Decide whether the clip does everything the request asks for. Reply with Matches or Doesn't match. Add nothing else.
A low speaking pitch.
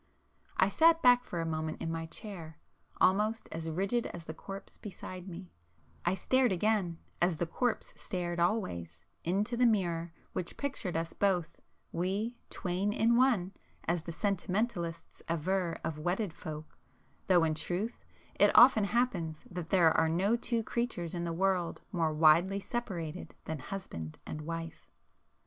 Doesn't match